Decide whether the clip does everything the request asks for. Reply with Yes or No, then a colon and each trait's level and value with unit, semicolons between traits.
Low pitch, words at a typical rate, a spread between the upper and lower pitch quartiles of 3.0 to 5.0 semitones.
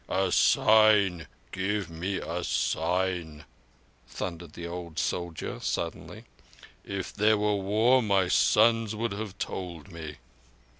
No: very low, 95 Hz; slow, 115 wpm; average, 3.6 semitones